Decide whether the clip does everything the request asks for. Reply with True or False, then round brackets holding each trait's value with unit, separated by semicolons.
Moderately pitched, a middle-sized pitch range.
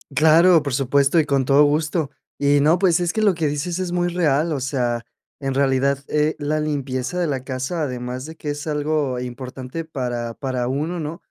True (145 Hz; 3.4 semitones)